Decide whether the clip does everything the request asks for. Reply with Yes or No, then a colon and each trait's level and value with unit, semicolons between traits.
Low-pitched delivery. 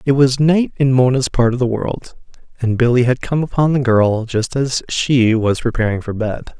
Yes: low, 125 Hz